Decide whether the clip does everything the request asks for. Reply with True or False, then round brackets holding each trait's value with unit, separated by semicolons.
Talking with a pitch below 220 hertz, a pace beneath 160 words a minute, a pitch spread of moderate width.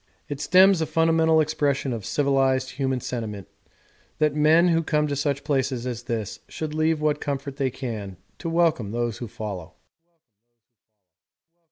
True (140 Hz; 150 wpm; 4.5 semitones)